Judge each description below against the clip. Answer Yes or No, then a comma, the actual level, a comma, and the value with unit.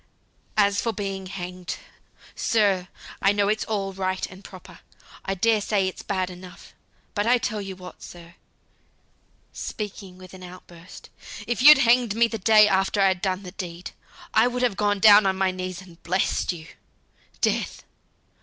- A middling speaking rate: Yes, average, 170 wpm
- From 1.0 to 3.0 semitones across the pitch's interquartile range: Yes, narrow, 2.4 semitones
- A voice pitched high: Yes, high, 195 Hz